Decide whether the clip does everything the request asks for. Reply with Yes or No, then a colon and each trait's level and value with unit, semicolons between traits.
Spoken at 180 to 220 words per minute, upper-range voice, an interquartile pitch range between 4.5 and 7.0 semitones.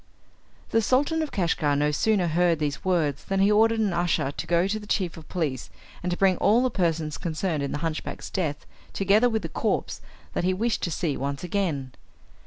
No: fast, 205 wpm; medium, 175 Hz; average, 4.9 semitones